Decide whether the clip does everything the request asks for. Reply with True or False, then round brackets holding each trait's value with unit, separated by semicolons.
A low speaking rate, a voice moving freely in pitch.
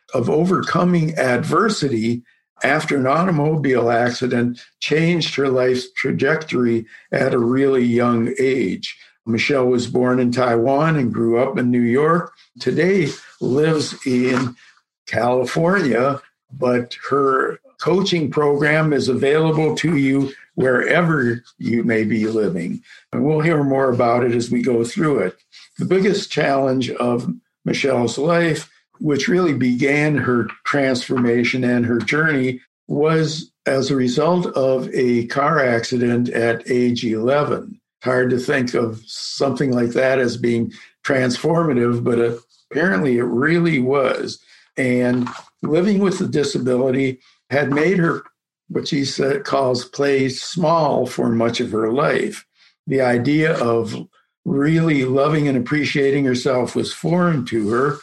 False (130 wpm; 3.7 semitones)